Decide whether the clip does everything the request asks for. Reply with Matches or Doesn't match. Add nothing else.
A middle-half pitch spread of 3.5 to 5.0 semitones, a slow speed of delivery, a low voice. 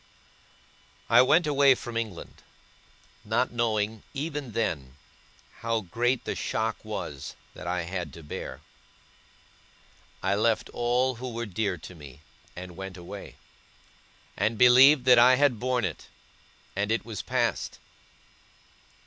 Matches